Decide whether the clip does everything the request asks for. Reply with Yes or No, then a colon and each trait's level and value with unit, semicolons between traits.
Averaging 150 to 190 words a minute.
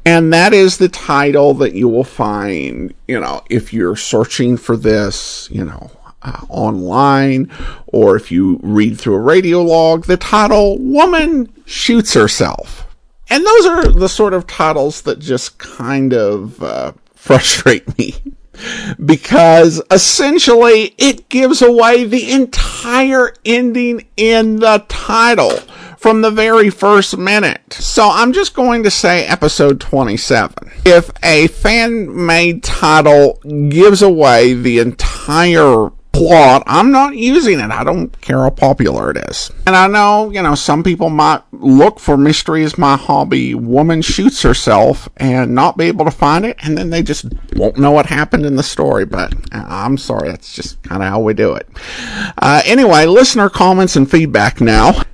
Yes: average, 160 wpm